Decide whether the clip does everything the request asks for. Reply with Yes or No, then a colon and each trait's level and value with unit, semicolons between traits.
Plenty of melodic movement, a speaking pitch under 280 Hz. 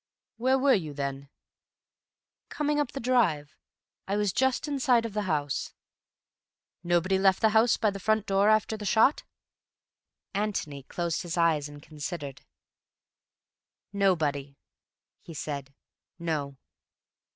Yes: wide, 6.9 semitones; high, 190 Hz